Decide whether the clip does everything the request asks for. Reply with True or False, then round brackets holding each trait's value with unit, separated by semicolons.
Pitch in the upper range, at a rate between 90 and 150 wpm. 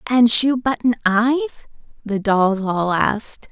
True (225 Hz; 135 wpm)